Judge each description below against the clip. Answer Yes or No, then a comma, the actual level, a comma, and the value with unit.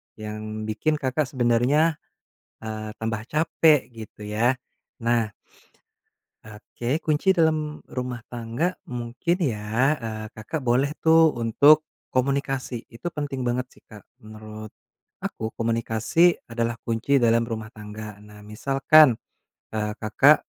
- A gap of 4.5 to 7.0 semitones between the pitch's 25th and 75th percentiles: Yes, average, 4.8 semitones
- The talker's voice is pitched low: Yes, low, 120 Hz